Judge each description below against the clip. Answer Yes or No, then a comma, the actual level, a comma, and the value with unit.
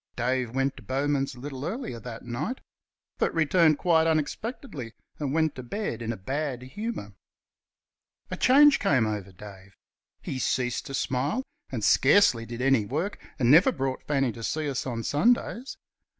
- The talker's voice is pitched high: No, low, 135 Hz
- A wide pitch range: No, average, 4.9 semitones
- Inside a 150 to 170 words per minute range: Yes, average, 165 wpm